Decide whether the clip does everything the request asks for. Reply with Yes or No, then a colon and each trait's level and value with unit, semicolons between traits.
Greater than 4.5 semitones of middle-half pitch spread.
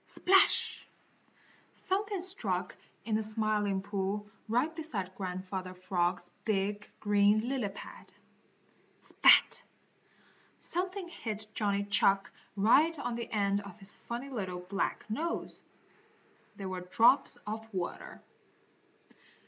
No: average, 4.0 semitones